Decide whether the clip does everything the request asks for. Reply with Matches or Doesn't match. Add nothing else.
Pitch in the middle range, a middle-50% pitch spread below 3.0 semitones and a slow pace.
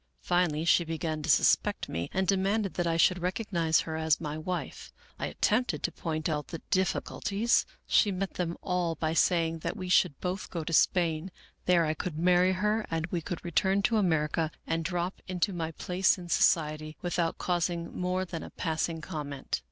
Doesn't match